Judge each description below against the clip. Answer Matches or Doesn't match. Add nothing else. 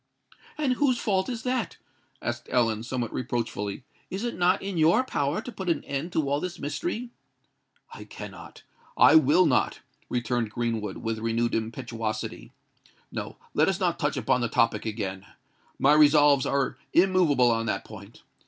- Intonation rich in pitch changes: Matches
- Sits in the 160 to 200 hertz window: Doesn't match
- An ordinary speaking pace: Matches